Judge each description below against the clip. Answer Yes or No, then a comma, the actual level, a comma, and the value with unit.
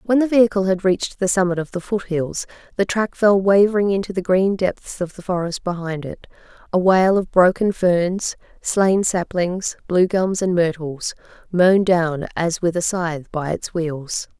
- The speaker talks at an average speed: Yes, average, 180 wpm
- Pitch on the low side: No, medium, 185 Hz